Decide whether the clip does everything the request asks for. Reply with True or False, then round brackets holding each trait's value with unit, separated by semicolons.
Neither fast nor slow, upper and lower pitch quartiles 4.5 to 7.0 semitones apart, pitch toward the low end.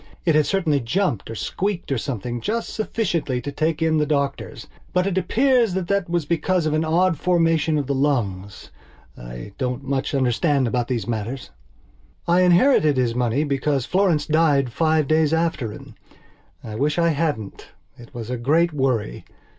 False (170 wpm; 5.3 semitones; 150 Hz)